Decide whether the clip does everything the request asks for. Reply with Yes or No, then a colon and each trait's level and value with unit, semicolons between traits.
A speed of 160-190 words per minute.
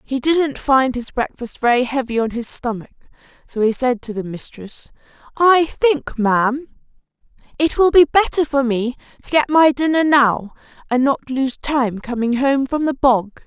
Yes: average, 175 wpm